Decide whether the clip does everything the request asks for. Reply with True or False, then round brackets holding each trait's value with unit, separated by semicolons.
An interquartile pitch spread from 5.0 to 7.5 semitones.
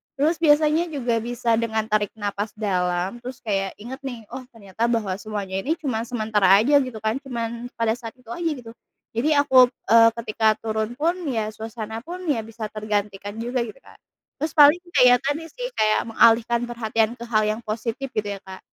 False (3.3 semitones)